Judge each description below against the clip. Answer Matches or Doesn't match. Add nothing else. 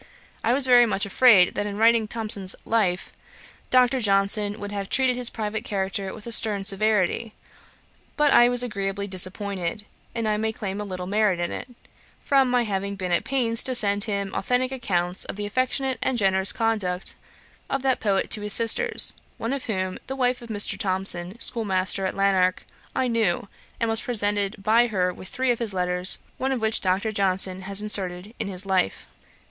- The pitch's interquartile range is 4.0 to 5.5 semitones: Doesn't match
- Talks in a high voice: Matches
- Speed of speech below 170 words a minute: Doesn't match